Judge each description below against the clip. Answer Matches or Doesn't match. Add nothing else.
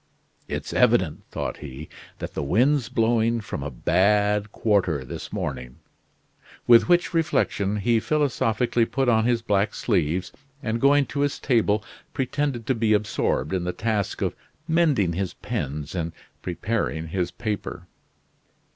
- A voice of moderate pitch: Doesn't match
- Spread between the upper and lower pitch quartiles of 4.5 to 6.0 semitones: Matches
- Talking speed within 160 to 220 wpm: Doesn't match